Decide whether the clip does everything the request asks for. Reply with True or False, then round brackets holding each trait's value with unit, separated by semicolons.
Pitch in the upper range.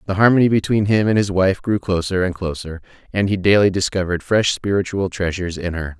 False (95 Hz)